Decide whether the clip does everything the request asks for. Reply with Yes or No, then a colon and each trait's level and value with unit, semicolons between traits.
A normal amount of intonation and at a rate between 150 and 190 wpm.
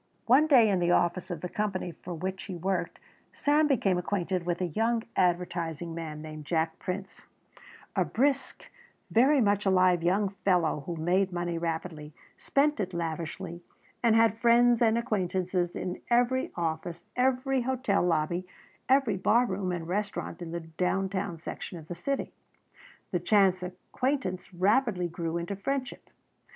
Yes: average, 4.7 semitones; average, 155 wpm